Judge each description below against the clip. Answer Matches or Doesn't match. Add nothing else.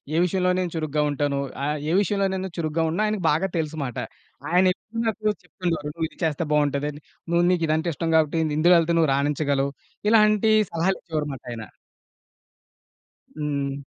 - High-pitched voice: Doesn't match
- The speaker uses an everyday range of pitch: Matches